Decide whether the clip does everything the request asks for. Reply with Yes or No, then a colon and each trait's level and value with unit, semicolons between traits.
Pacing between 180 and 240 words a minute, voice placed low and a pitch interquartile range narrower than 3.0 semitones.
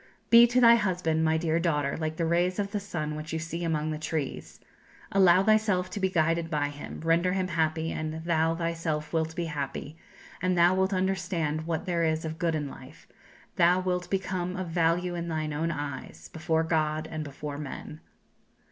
No: average, 190 wpm; medium, 165 Hz; narrow, 2.5 semitones